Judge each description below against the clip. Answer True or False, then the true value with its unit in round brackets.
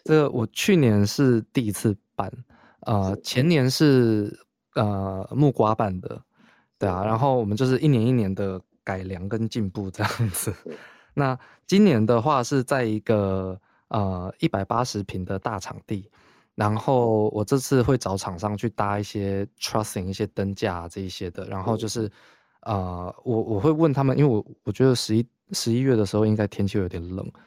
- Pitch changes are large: False (4.2 semitones)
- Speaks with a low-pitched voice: True (110 Hz)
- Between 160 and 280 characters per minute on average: True (265 characters per minute)